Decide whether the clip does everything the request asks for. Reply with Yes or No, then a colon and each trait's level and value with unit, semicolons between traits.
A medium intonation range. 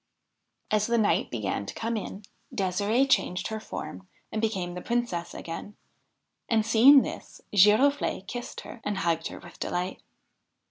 Yes: average, 4.3 semitones